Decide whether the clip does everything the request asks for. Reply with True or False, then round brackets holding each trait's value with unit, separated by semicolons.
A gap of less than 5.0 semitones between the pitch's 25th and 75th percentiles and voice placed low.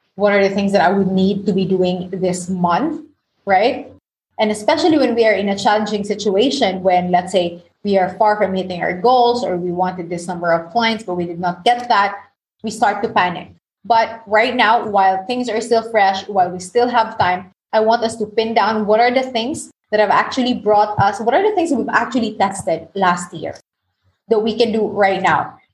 False (3.7 semitones; 205 Hz)